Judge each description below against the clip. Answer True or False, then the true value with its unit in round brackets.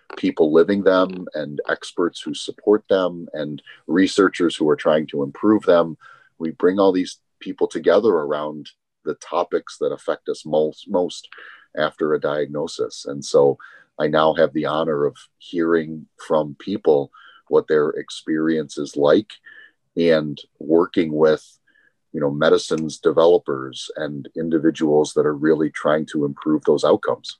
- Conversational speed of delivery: True (145 wpm)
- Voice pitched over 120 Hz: False (95 Hz)